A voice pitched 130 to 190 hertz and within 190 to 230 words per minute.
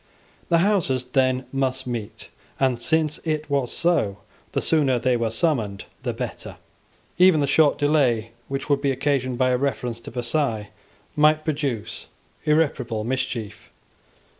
No: low, 135 Hz; average, 140 wpm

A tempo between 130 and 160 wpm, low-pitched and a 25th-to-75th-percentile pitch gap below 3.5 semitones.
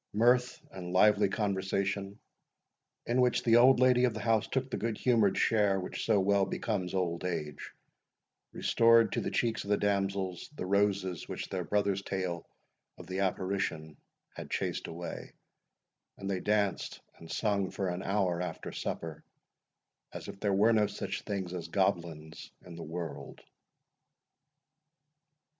Yes: average, 150 wpm; low, 100 Hz; average, 2.9 semitones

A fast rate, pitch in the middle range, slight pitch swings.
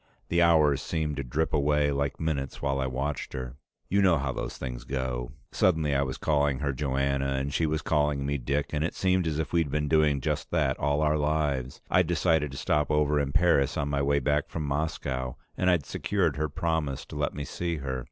No: fast, 220 wpm; very low, 75 Hz; narrow, 2.2 semitones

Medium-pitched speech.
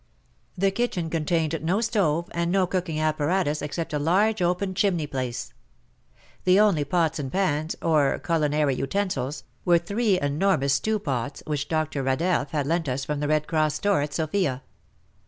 Yes: medium, 160 Hz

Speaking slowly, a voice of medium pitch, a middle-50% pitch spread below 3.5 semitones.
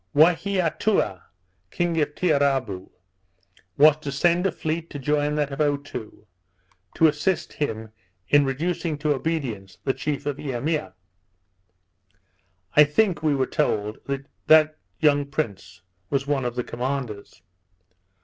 Yes: slow, 125 wpm; medium, 145 Hz; average, 3.1 semitones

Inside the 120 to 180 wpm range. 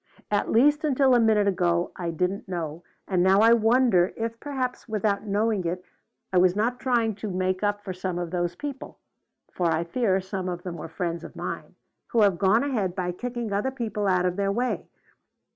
No: average, 200 wpm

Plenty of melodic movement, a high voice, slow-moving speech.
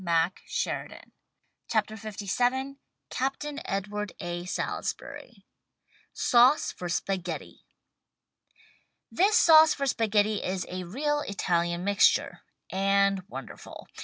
Yes: wide, 6.1 semitones; high, 205 Hz; slow, 105 wpm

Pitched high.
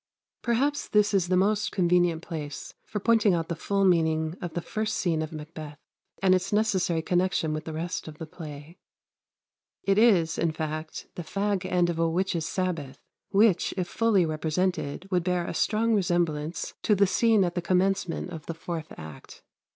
No: medium, 175 Hz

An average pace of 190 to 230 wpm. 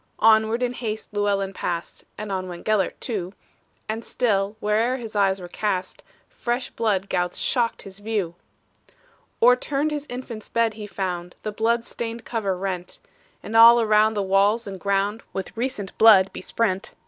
No: average, 160 wpm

